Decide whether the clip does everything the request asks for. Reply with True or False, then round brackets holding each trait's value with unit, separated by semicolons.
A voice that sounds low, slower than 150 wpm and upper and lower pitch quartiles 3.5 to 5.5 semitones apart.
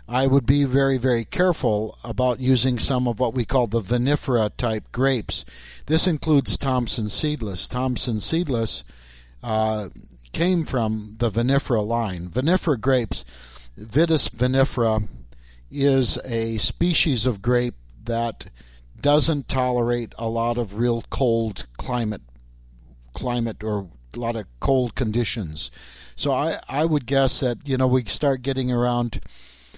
True (120 Hz; 135 wpm; 3.9 semitones)